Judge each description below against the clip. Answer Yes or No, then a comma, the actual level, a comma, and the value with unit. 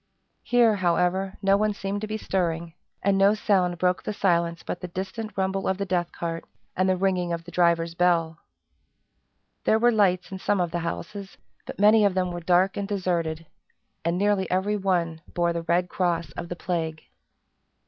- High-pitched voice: No, medium, 180 Hz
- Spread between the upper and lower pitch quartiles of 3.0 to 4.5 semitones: No, narrow, 2.5 semitones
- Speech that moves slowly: No, average, 190 wpm